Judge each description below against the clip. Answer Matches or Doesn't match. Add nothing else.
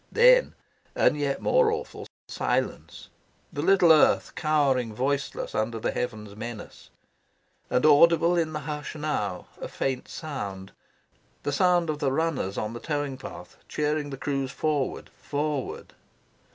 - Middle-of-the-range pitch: Matches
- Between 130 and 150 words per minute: Matches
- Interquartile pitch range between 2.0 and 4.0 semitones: Matches